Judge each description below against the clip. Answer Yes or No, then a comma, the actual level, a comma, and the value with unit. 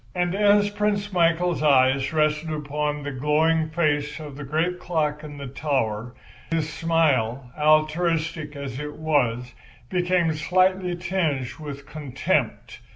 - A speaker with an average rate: No, slow, 130 wpm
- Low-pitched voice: No, medium, 155 Hz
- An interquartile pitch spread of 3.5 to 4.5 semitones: No, average, 3.0 semitones